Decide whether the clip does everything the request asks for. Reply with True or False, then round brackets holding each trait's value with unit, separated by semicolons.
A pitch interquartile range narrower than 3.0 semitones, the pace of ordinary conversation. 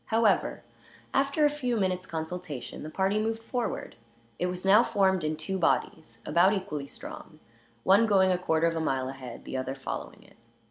False (5.0 semitones; 180 wpm)